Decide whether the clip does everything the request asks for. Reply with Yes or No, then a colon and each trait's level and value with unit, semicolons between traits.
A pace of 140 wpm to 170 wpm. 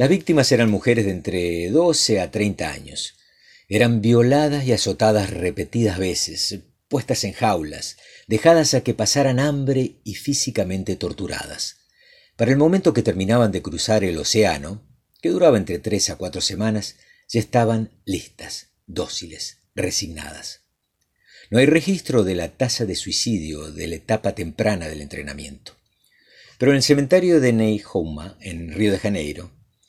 Yes: average, 145 wpm